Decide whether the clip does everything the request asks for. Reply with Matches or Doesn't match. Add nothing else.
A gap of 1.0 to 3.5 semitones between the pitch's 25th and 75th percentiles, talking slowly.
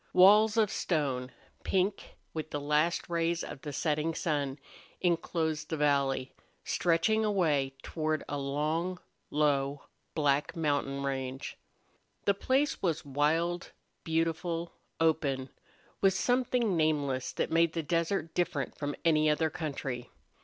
Matches